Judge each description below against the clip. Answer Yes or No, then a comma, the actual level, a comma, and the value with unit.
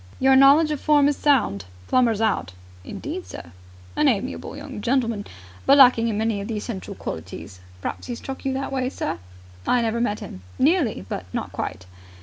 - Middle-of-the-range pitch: No, high, 235 Hz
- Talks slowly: No, average, 180 wpm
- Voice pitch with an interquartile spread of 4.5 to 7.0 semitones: Yes, average, 5.0 semitones